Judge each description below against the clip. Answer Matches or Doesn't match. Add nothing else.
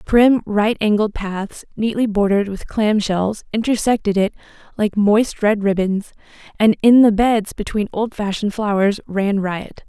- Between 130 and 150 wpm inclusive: Matches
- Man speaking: Doesn't match